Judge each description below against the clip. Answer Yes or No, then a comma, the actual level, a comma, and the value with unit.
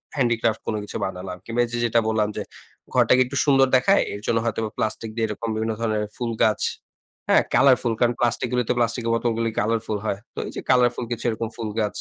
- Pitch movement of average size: No, narrow, 1.8 semitones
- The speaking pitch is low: Yes, low, 115 Hz